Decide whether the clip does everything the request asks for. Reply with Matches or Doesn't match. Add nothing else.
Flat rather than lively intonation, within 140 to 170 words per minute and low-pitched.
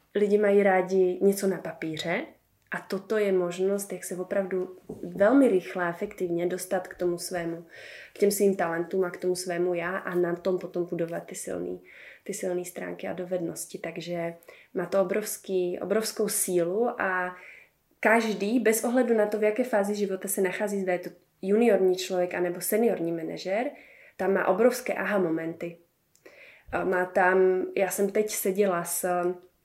Doesn't match